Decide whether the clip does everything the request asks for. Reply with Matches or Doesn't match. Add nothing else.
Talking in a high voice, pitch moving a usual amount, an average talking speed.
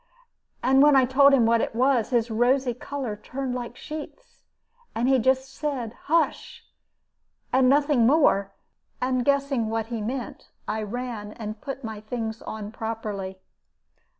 Matches